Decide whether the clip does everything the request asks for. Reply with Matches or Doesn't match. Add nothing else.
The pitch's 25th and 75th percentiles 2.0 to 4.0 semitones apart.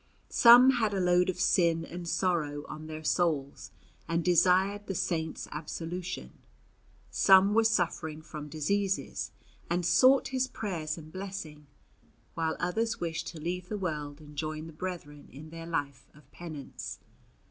Matches